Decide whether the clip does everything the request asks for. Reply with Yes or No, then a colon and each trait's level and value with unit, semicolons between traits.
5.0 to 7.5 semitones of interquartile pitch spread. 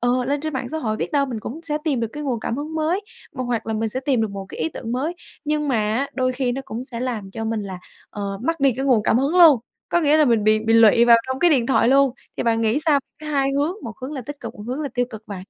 No: average, 4.2 semitones